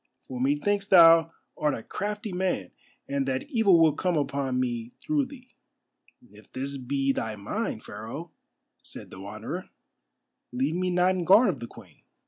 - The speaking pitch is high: No, medium, 145 Hz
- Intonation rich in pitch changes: Yes, wide, 6.8 semitones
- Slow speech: No, average, 160 wpm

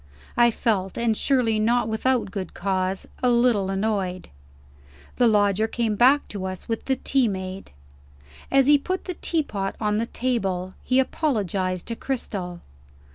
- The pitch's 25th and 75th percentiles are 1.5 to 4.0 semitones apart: No, average, 4.4 semitones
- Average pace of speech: Yes, average, 150 wpm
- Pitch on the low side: No, high, 220 Hz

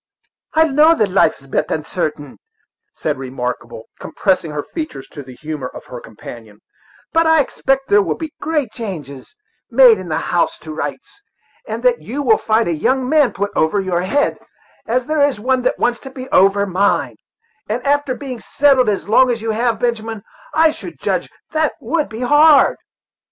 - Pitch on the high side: Yes, high, 230 Hz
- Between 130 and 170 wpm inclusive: No, average, 185 wpm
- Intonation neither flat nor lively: No, wide, 8.2 semitones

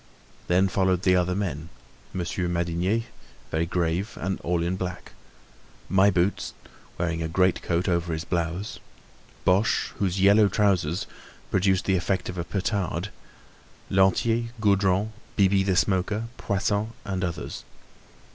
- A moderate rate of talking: No, slow, 130 wpm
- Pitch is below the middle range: Yes, very low, 95 Hz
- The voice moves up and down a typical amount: No, narrow, 2.3 semitones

